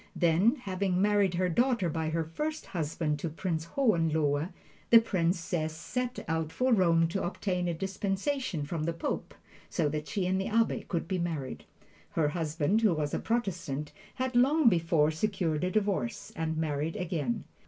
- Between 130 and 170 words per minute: Yes, average, 165 wpm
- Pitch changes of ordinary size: Yes, average, 4.1 semitones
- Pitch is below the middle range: No, medium, 175 Hz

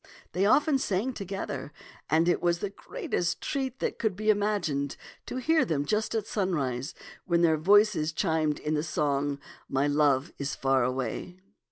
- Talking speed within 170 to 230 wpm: Yes, average, 175 wpm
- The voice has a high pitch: No, medium, 170 Hz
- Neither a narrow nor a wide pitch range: No, wide, 6.3 semitones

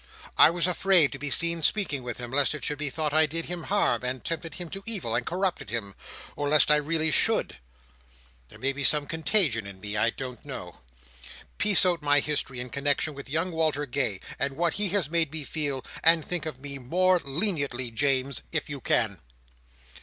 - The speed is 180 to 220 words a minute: Yes, fast, 205 wpm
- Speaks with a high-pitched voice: No, medium, 150 Hz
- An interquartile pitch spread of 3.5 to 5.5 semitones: Yes, average, 3.8 semitones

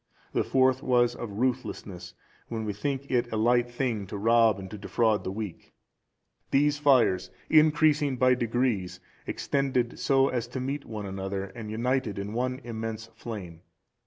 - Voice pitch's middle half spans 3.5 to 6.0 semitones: Yes, average, 3.8 semitones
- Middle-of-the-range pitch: No, low, 120 Hz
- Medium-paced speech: Yes, average, 160 wpm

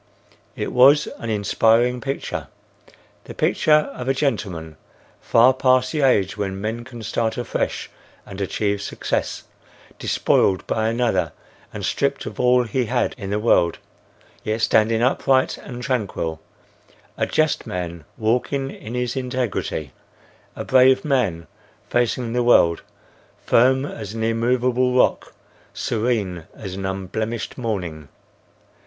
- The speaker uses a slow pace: Yes, slow, 130 wpm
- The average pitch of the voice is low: Yes, low, 115 Hz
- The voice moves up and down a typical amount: Yes, average, 4.2 semitones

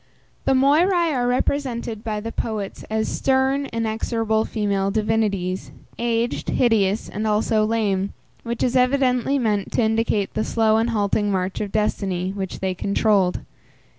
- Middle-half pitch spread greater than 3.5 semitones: No, average, 2.9 semitones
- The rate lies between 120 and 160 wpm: Yes, average, 140 wpm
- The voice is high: Yes, high, 220 Hz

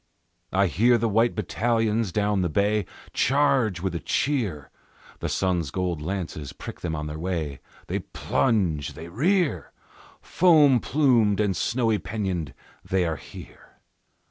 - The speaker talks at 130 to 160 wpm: Yes, average, 140 wpm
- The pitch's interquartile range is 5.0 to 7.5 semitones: Yes, wide, 5.4 semitones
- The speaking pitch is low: Yes, low, 100 Hz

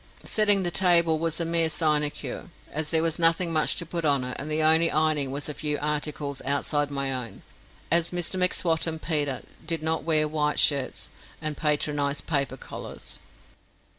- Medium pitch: Yes, medium, 155 Hz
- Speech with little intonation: Yes, narrow, 2.1 semitones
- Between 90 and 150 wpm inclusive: No, average, 175 wpm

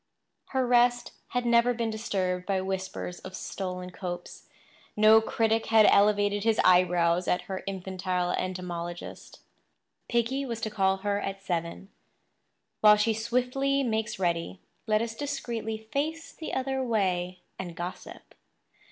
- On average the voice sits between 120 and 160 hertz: No, high, 205 Hz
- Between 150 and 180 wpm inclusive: No, slow, 135 wpm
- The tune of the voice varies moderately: Yes, average, 4.3 semitones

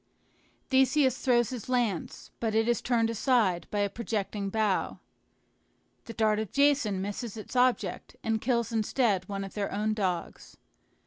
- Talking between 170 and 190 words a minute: No, average, 150 wpm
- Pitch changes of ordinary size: Yes, average, 3.1 semitones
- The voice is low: No, high, 220 Hz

